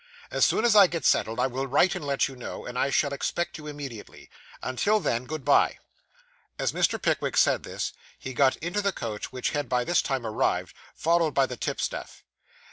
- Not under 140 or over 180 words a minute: No, fast, 205 wpm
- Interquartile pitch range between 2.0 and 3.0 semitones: No, average, 4.6 semitones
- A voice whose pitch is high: No, medium, 140 Hz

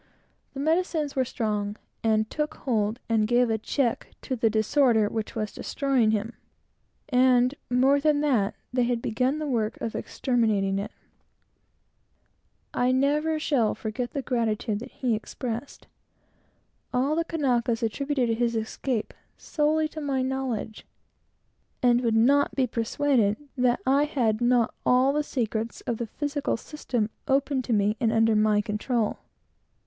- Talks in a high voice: Yes, high, 245 Hz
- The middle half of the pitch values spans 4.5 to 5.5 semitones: No, average, 3.7 semitones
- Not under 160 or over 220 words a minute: No, average, 145 wpm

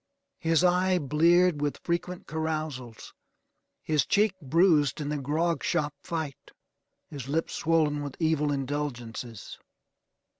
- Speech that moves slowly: Yes, slow, 115 wpm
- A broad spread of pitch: No, average, 2.7 semitones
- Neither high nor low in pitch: Yes, medium, 155 Hz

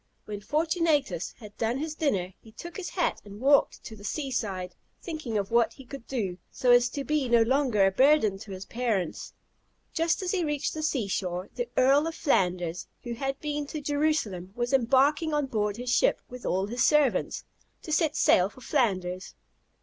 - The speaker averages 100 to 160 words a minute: No, average, 195 wpm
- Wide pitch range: Yes, wide, 6.6 semitones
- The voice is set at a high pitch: Yes, very high, 250 Hz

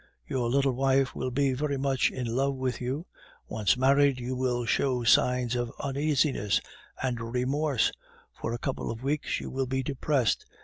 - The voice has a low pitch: Yes, low, 130 Hz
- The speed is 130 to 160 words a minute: No, average, 170 wpm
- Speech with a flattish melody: Yes, narrow, 2.0 semitones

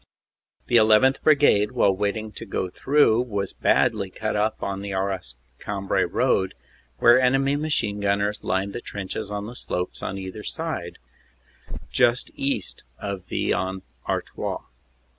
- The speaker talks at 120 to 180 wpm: Yes, average, 150 wpm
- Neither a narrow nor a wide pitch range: Yes, average, 3.6 semitones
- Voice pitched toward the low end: Yes, low, 105 Hz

